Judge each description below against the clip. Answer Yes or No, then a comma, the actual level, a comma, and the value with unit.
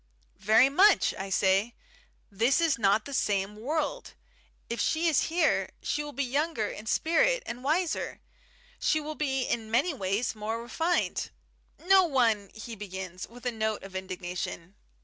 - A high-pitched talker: Yes, high, 235 Hz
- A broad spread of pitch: Yes, wide, 6.9 semitones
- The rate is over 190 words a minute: No, average, 165 wpm